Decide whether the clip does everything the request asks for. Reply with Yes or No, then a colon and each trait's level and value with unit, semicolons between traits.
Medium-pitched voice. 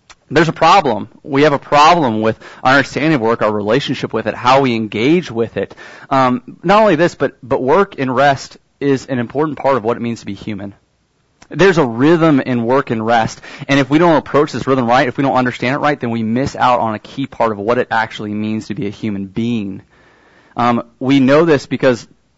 No: low, 130 Hz